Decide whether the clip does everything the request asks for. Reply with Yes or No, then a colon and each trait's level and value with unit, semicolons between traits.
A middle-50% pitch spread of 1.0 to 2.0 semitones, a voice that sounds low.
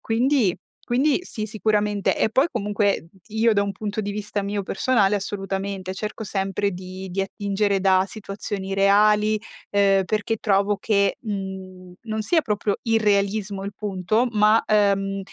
No: narrow, 1.7 semitones; high, 205 Hz